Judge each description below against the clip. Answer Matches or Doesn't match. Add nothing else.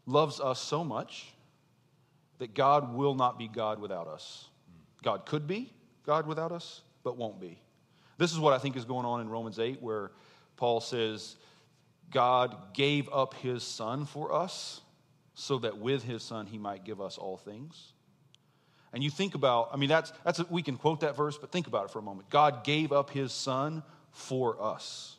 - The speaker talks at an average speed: Matches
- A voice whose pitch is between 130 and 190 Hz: Matches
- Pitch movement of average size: Matches